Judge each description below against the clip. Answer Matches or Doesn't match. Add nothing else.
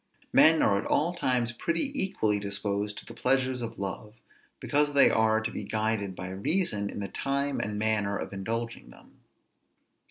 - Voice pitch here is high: Doesn't match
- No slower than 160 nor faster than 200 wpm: Matches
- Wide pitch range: Doesn't match